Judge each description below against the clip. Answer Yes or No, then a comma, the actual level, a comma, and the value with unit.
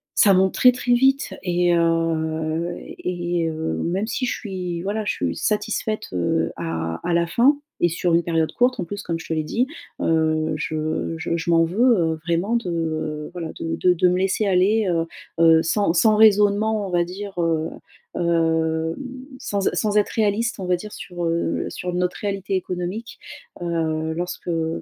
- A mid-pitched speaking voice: Yes, medium, 175 Hz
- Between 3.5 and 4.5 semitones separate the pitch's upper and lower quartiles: Yes, average, 3.8 semitones